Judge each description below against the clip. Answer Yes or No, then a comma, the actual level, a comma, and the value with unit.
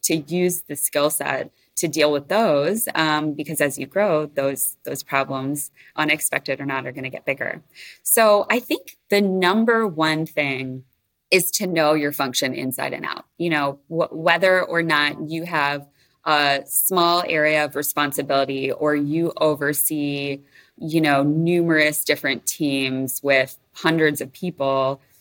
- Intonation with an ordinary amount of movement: Yes, average, 3.4 semitones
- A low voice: No, medium, 150 Hz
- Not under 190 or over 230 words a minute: No, average, 155 wpm